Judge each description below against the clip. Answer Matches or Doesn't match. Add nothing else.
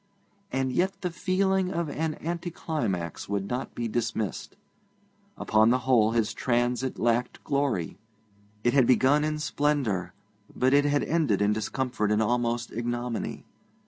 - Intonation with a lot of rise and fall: Doesn't match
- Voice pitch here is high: Doesn't match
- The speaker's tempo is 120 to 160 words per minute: Matches